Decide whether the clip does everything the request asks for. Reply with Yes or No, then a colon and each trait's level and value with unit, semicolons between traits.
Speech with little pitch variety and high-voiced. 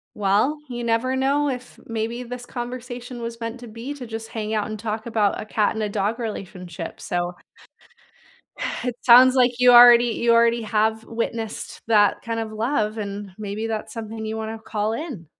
Yes: narrow, 2.1 semitones; high, 225 Hz